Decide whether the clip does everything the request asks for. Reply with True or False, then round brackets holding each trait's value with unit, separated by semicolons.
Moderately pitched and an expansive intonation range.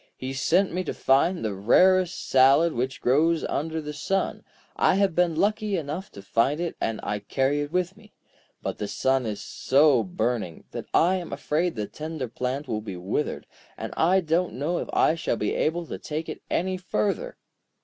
True (150 Hz; 6.0 semitones)